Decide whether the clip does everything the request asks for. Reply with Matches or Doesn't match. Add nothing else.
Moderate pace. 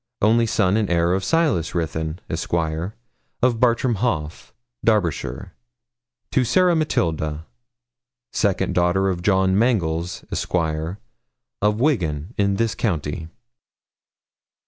Doesn't match